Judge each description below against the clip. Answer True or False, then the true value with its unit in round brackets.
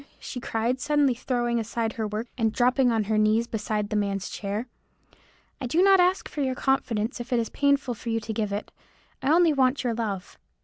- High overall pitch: True (235 Hz)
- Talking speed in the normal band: False (210 wpm)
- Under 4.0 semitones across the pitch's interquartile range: True (3.5 semitones)